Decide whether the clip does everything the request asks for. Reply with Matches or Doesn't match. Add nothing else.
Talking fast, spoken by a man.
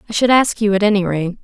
Doesn't match